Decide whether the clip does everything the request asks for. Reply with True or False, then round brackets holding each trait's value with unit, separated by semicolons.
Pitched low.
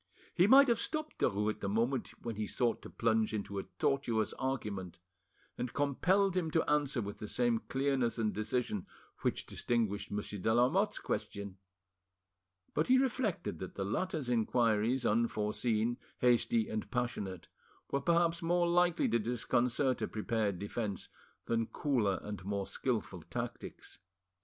True (120 Hz)